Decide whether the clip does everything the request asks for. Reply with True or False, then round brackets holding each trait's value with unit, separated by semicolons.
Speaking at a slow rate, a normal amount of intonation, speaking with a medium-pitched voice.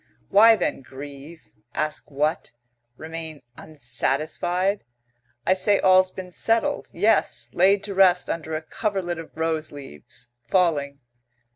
True (120 wpm; 4.2 semitones; 165 Hz)